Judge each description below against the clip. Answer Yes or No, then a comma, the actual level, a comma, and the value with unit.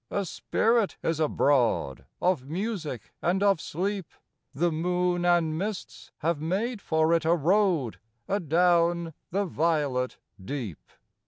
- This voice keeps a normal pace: No, slow, 120 wpm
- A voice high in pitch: No, medium, 170 Hz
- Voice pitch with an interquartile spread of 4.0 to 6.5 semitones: No, average, 3.5 semitones